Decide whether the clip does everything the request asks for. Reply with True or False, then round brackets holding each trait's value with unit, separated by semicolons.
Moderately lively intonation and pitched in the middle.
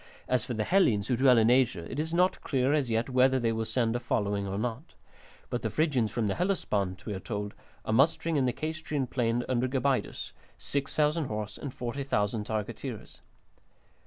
False (4.3 semitones; 125 Hz)